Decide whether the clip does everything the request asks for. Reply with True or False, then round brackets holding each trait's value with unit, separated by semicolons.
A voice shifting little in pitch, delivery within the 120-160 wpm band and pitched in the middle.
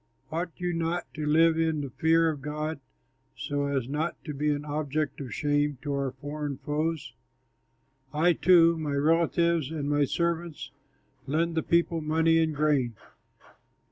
True (2.2 semitones; 155 wpm; 155 Hz)